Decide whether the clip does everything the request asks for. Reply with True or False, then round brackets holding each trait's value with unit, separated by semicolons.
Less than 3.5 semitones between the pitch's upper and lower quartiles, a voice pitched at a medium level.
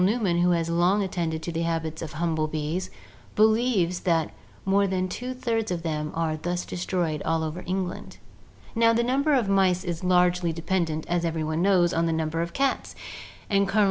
True (3.1 semitones; 175 Hz)